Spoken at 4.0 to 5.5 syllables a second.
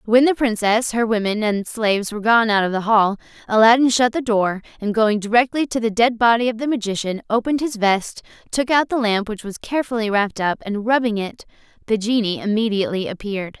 No: 5.8 syllables/s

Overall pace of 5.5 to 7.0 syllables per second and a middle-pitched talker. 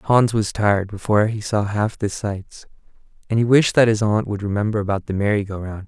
No: 5.6 syllables/s; low, 105 Hz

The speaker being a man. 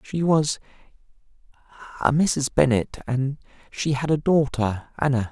Yes: male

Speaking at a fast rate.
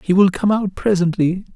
No: average, 195 wpm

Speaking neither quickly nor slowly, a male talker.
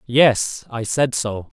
Yes: average, 150 wpm; male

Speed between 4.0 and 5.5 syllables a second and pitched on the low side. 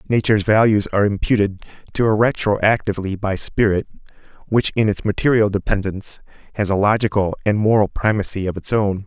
No: 5.8 syllables/s; low, 105 Hz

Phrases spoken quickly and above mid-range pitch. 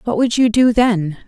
Yes: fast, 235 wpm; high, 220 Hz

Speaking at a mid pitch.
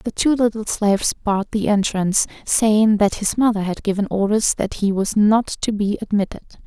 No: high, 210 Hz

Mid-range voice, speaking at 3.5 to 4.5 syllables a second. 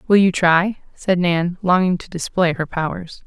Yes: medium, 175 Hz; 4.4 syllables/s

